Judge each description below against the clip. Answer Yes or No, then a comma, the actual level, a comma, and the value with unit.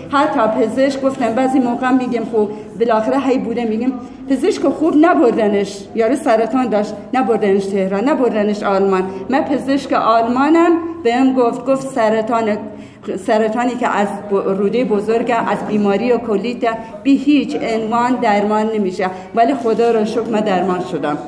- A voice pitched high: Yes, high, 230 Hz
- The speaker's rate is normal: Yes, average, 135 wpm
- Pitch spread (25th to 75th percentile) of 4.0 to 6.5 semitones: No, average, 3.6 semitones